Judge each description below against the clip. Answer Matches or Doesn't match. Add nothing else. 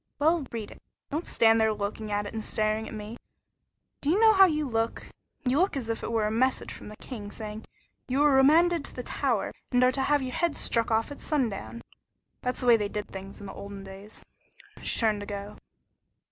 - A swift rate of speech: Matches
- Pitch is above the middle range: Matches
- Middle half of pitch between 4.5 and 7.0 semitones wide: Matches